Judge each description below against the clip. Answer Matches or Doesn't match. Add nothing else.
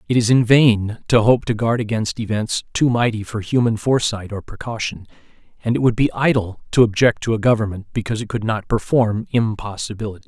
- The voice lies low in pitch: Matches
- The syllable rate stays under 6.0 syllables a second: Matches